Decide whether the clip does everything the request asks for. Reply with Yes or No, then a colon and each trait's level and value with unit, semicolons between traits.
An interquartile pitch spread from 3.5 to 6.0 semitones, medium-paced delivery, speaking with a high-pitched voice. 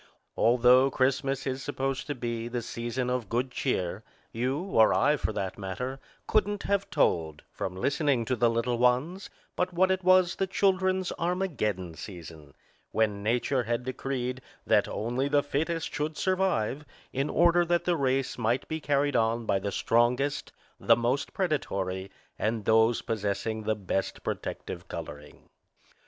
No: average, 5.0 semitones; average, 150 wpm; low, 125 Hz